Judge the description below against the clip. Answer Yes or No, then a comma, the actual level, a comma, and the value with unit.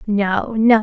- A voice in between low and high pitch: No, high, 210 Hz